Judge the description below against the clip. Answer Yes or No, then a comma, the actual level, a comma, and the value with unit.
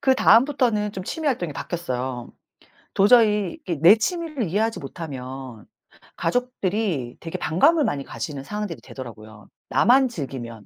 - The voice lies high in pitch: No, medium, 180 Hz